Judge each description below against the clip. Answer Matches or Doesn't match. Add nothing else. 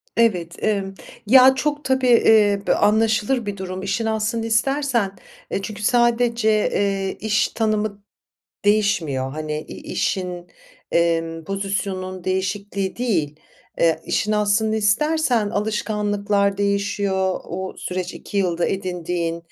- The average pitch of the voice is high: Matches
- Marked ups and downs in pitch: Doesn't match